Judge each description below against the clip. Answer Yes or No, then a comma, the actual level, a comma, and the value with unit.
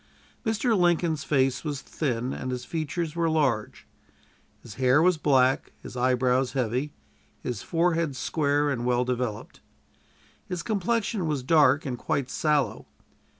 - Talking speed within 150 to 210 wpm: No, slow, 135 wpm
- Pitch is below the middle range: No, medium, 145 Hz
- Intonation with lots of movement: No, average, 4.6 semitones